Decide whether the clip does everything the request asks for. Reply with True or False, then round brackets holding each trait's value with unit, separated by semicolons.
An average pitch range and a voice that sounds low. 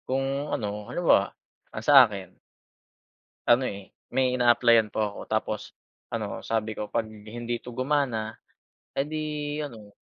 True (3.3 semitones; 115 Hz)